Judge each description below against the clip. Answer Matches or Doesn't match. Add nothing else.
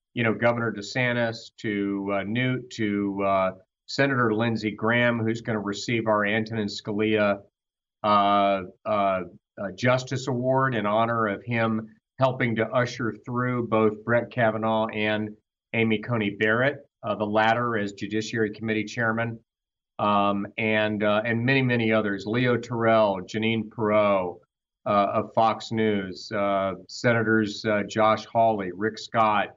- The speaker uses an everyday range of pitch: Doesn't match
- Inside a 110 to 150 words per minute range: Matches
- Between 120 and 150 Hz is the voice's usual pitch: Doesn't match